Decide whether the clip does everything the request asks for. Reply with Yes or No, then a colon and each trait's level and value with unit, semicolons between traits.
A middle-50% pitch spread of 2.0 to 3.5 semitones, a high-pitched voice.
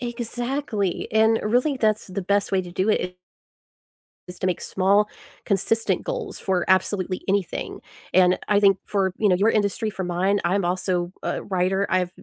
Yes: average, 2.7 semitones; high, 195 Hz